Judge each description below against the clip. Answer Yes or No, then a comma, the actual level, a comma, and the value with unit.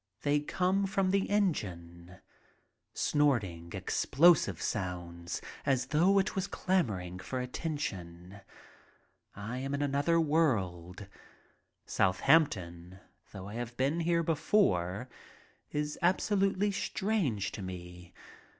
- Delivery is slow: Yes, slow, 105 wpm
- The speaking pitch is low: Yes, low, 130 Hz